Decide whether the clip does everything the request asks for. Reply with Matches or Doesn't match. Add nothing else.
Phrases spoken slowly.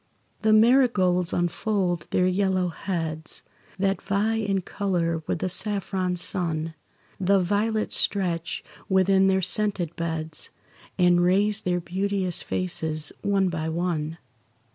Matches